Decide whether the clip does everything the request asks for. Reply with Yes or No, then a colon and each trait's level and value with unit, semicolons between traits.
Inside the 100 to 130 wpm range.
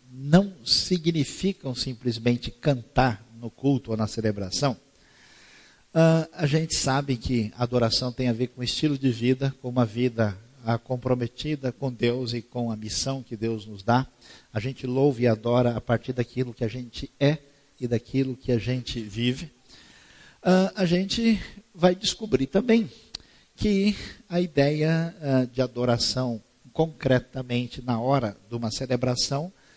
No: average, 145 wpm